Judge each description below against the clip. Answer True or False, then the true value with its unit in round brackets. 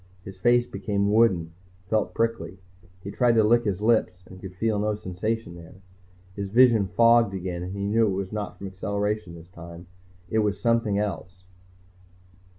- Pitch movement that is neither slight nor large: True (3.3 semitones)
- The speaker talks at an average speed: True (170 wpm)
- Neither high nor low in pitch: False (100 Hz)